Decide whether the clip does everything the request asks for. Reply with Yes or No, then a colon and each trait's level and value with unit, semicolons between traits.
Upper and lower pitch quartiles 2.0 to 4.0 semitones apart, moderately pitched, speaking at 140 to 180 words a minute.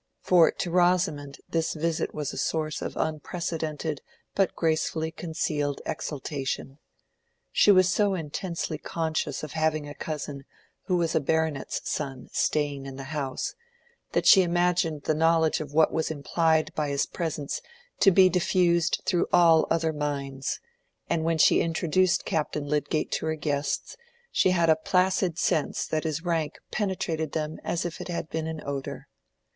Yes: narrow, 2.5 semitones; medium, 160 Hz; average, 155 wpm